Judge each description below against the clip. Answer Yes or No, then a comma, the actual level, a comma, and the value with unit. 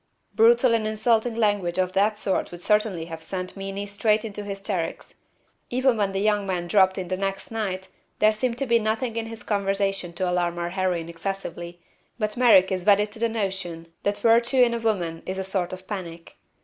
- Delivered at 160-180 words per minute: No, average, 200 wpm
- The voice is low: No, high, 195 Hz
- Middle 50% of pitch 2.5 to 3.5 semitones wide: Yes, average, 3.1 semitones